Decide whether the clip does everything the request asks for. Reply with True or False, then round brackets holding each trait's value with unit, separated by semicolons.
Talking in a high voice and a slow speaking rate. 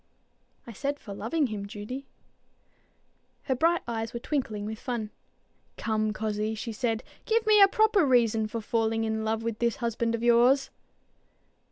False (230 Hz; 160 wpm)